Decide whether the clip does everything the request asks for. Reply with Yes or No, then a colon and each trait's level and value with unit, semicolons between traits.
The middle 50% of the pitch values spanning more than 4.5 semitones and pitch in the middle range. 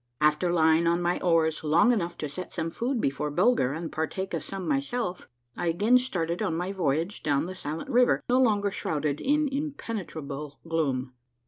Yes: average, 5.2 semitones; medium, 170 Hz